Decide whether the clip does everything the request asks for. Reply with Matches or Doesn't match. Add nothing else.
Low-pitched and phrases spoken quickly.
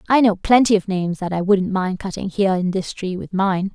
Doesn't match